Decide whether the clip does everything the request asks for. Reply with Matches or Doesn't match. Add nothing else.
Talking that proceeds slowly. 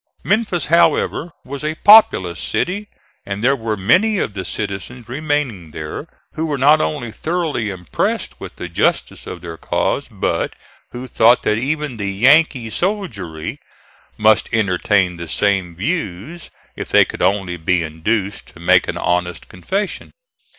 Doesn't match